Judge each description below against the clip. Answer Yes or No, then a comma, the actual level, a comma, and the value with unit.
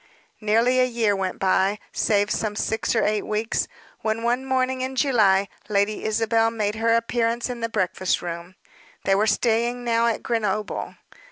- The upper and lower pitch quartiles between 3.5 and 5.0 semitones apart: No, narrow, 2.4 semitones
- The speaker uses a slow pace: No, average, 165 wpm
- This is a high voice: Yes, high, 225 Hz